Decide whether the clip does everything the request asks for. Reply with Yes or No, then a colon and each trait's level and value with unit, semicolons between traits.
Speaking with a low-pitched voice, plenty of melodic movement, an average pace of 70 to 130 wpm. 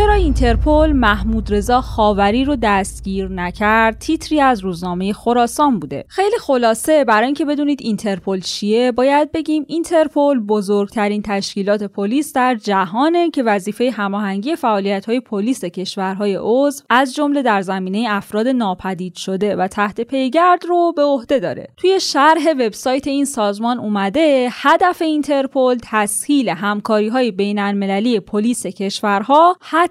No: high, 230 Hz; wide, 5.9 semitones; average, 125 wpm